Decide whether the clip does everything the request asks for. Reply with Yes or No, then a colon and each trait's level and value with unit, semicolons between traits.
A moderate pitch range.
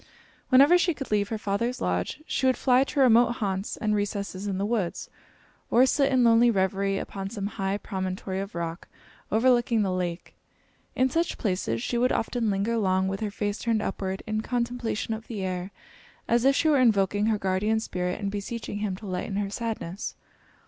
Yes: average, 3.6 semitones